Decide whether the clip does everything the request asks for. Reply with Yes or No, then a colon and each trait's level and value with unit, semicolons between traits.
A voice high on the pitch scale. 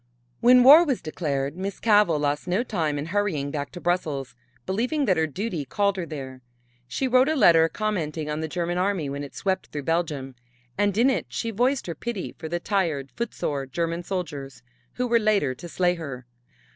No: medium, 175 Hz